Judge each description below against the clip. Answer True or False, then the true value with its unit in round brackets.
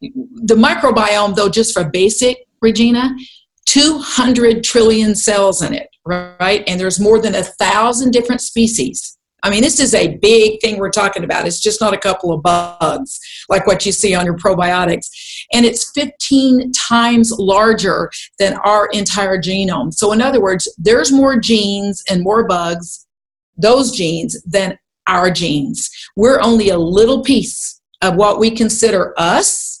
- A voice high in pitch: True (215 Hz)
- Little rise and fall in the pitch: False (3.8 semitones)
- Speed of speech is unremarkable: True (160 wpm)